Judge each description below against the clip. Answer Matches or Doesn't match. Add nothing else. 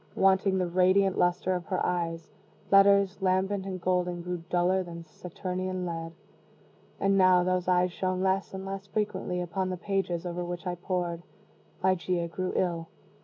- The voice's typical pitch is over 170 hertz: Matches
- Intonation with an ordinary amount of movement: Doesn't match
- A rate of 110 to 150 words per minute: Doesn't match